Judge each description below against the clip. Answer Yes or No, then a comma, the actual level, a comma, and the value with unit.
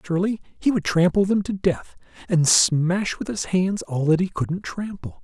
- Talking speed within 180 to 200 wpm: Yes, average, 195 wpm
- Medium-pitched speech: Yes, medium, 180 Hz